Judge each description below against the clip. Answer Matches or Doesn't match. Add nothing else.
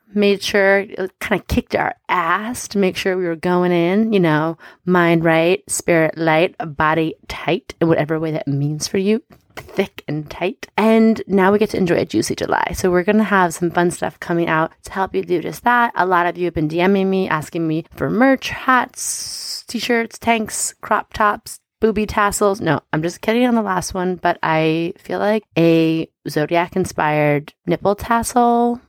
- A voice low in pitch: Doesn't match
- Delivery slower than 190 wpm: Doesn't match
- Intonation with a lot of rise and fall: Doesn't match